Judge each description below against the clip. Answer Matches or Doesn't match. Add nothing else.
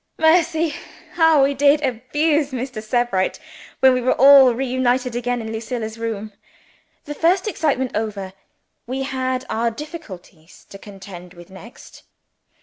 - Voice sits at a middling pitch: Doesn't match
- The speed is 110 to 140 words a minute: Matches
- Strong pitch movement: Doesn't match